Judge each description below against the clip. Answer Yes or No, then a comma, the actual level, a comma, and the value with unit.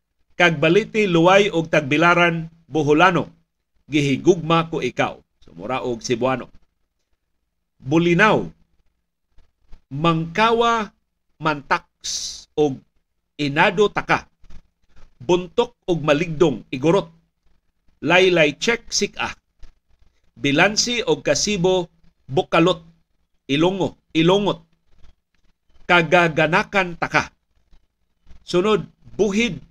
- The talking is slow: Yes, slow, 70 wpm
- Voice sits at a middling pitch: Yes, medium, 160 Hz